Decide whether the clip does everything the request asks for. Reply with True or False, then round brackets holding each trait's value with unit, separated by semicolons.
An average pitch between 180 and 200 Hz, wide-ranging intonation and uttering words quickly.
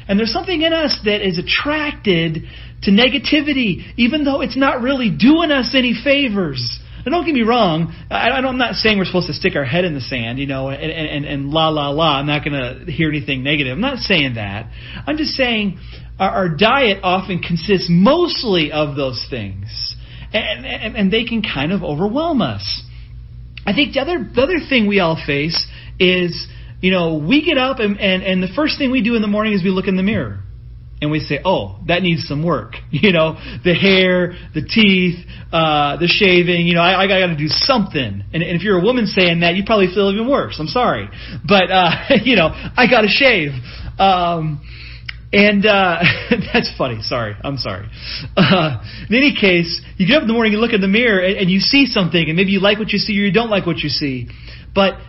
True (185 Hz; 6.8 semitones; 220 wpm)